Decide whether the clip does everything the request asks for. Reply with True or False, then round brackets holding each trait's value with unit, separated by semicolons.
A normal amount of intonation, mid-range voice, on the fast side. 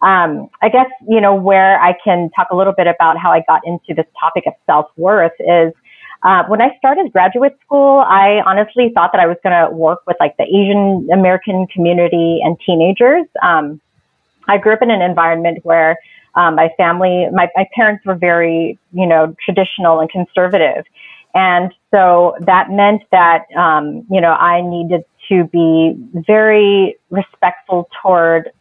False (3.0 semitones; 180 Hz; 170 wpm)